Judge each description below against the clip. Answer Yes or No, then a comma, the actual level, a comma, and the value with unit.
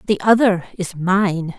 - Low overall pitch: No, high, 190 Hz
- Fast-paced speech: No, average, 150 wpm